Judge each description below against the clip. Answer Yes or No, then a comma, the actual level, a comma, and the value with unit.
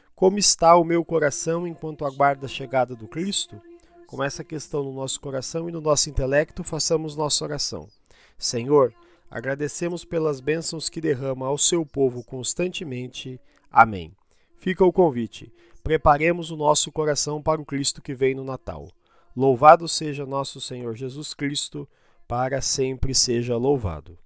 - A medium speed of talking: Yes, average, 145 wpm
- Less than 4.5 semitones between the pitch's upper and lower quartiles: Yes, average, 3.7 semitones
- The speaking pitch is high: No, medium, 145 Hz